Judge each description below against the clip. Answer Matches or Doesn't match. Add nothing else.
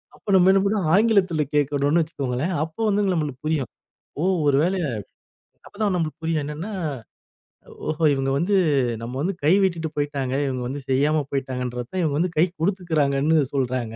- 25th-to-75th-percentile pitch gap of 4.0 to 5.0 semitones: Matches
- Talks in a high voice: Doesn't match